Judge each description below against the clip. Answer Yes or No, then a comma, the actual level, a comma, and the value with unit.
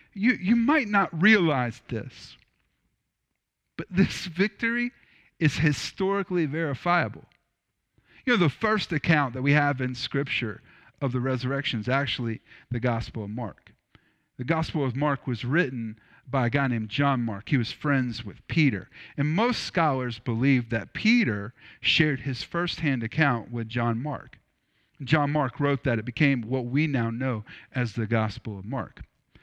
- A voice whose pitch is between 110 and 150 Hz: Yes, low, 135 Hz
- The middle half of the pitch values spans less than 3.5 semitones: No, average, 5.1 semitones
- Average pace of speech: Yes, average, 155 wpm